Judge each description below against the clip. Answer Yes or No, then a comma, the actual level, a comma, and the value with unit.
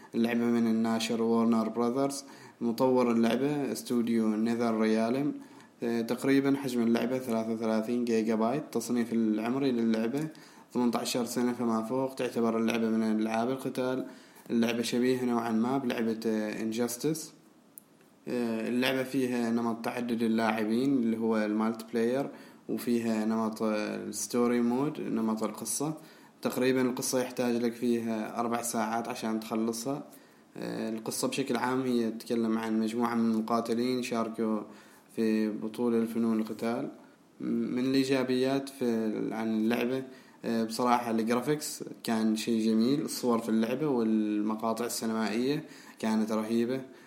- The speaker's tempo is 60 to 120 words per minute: Yes, average, 115 wpm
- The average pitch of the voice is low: Yes, low, 115 Hz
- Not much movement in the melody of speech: Yes, narrow, 1.9 semitones